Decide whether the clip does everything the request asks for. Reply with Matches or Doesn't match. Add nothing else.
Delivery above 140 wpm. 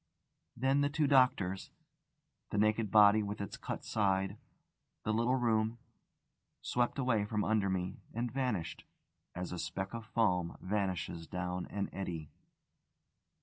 Doesn't match